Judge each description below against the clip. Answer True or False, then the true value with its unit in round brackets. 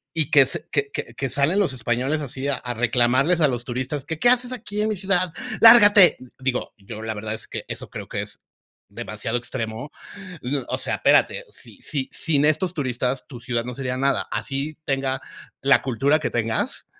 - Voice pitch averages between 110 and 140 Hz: True (135 Hz)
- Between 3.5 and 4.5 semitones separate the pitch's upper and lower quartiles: True (4.1 semitones)